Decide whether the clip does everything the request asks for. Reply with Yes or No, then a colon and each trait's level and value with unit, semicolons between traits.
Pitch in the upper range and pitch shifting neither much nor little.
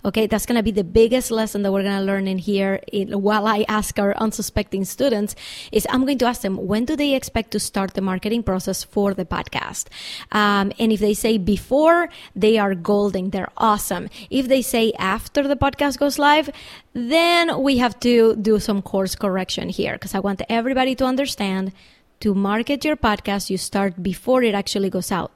Yes: high, 210 Hz; average, 3.9 semitones